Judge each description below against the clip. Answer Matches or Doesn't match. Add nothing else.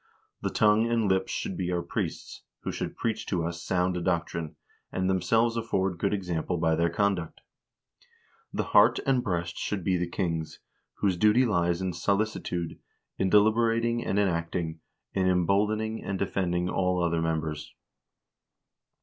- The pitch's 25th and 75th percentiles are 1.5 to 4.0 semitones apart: Matches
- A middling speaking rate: Matches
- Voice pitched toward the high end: Doesn't match